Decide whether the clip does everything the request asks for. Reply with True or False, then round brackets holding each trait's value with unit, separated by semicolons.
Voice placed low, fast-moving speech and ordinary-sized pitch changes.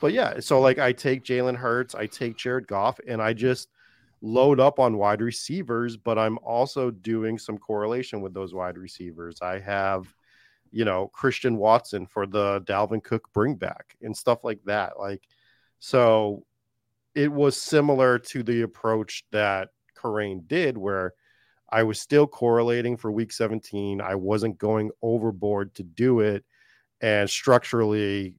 False (110 Hz; 155 wpm; 3.2 semitones)